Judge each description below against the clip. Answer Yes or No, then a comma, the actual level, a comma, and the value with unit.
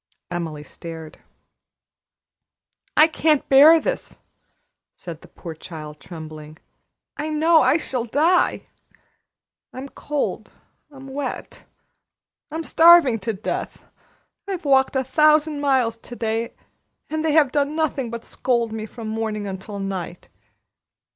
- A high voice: Yes, very high, 255 Hz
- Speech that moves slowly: Yes, slow, 120 wpm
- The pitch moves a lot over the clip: Yes, wide, 7.3 semitones